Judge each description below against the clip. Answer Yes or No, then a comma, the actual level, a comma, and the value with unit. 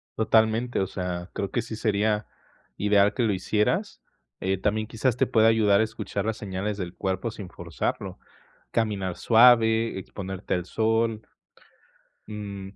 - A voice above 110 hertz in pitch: No, low, 105 Hz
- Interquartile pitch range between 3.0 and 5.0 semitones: No, narrow, 2.5 semitones